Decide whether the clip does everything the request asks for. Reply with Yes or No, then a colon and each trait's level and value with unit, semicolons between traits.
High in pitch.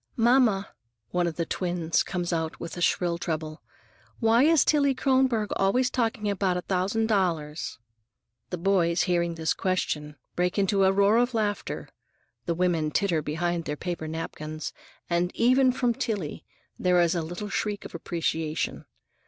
No: medium, 180 Hz